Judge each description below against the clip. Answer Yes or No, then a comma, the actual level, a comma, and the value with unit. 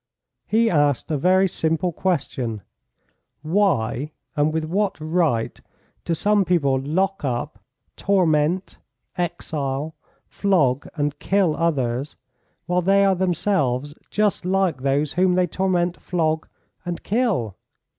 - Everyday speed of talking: No, slow, 115 wpm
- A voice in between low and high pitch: Yes, medium, 165 Hz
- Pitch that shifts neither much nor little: Yes, average, 4.6 semitones